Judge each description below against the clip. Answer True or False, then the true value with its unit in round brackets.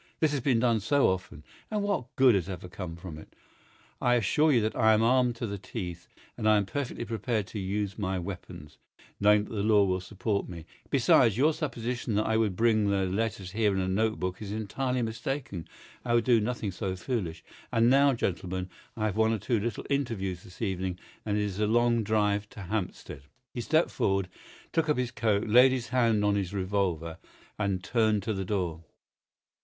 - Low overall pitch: True (105 Hz)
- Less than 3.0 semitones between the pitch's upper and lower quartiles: False (3.8 semitones)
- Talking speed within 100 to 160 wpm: False (205 wpm)